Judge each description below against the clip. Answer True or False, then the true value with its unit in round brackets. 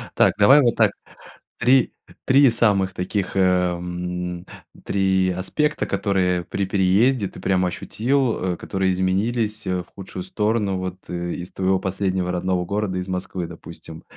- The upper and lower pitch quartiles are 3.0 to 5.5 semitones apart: False (2.5 semitones)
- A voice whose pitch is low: True (95 Hz)